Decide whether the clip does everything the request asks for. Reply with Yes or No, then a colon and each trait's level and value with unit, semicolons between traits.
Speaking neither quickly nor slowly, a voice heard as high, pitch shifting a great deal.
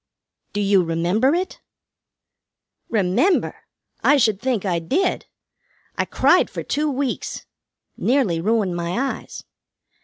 No: slow, 115 wpm; high, 215 Hz; wide, 7.1 semitones